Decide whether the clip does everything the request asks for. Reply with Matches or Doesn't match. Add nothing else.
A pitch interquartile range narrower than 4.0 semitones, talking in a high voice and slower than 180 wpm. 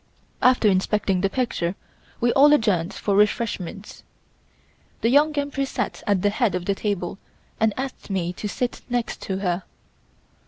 Doesn't match